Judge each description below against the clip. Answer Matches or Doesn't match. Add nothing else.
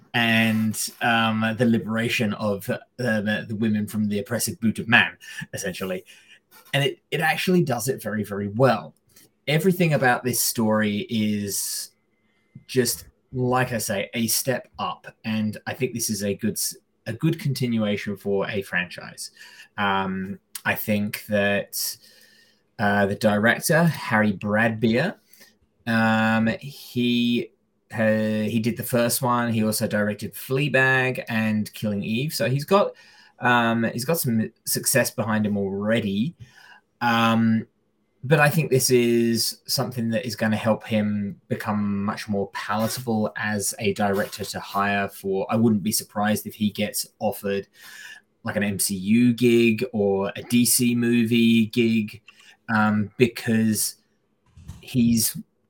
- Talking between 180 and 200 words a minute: Doesn't match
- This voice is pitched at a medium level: Doesn't match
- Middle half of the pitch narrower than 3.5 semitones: Matches